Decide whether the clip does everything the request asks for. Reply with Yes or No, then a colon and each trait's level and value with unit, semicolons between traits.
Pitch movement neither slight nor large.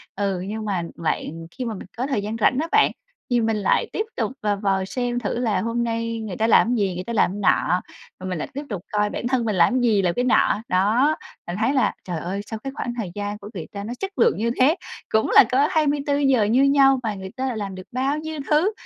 Yes: average, 4.6 semitones